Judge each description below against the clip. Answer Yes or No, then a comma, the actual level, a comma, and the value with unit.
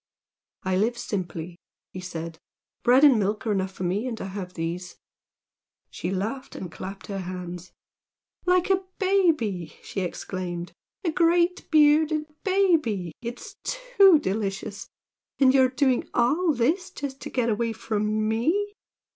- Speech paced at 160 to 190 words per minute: No, average, 140 wpm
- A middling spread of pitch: No, wide, 8.5 semitones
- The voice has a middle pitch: No, high, 225 Hz